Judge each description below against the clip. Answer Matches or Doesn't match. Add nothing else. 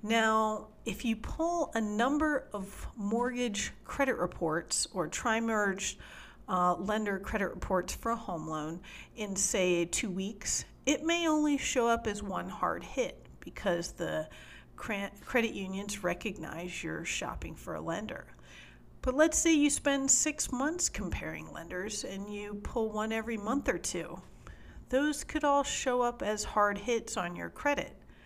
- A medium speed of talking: Matches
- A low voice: Doesn't match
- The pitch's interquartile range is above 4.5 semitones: Matches